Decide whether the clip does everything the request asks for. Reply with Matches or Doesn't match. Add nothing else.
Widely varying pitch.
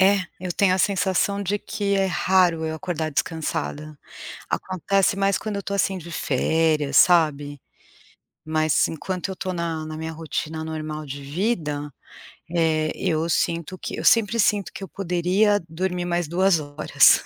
Doesn't match